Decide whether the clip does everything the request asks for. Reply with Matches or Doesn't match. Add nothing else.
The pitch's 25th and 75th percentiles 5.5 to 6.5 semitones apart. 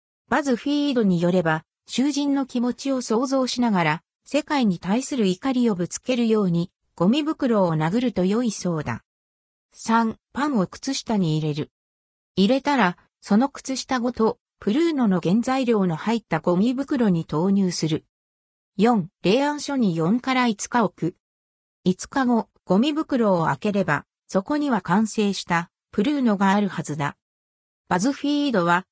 Doesn't match